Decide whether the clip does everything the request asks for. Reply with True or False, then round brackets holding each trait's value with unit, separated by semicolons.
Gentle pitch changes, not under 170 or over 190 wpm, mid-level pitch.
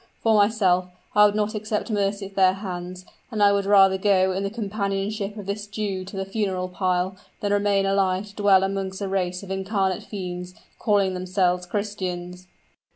False (1.8 semitones; 180 wpm; 195 Hz)